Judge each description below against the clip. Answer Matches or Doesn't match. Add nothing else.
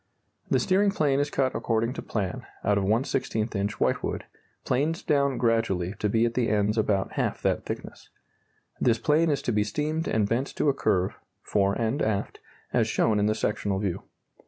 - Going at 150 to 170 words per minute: Doesn't match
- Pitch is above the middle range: Doesn't match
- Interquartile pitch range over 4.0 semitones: Matches